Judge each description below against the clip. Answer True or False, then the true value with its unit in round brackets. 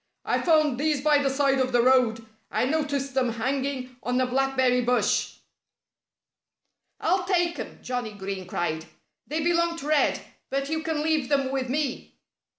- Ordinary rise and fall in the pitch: True (3.4 semitones)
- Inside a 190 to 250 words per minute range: False (160 wpm)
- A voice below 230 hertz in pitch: False (270 Hz)